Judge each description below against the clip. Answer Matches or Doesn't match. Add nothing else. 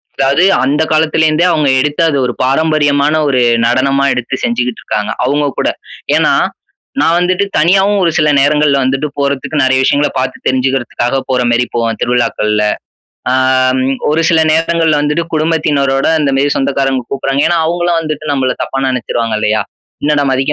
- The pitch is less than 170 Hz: Matches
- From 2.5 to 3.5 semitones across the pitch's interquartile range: Matches